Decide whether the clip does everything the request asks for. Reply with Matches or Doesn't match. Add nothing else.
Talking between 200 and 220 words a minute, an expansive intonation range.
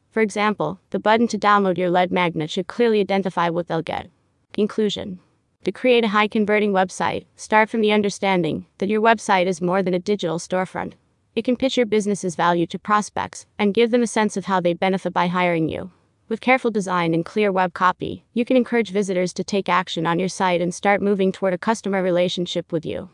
Doesn't match